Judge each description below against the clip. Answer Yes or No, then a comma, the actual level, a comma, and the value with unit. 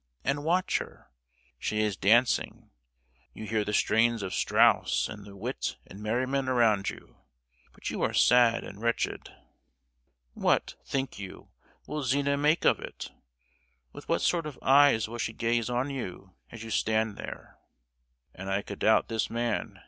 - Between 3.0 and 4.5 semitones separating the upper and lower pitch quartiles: Yes, average, 3.8 semitones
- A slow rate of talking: No, average, 160 wpm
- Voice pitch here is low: Yes, low, 115 Hz